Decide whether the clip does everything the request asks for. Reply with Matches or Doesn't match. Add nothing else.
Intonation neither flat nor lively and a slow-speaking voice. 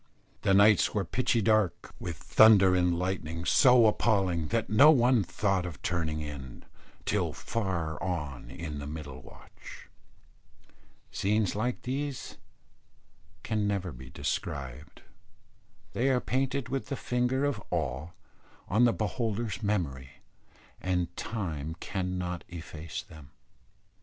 Doesn't match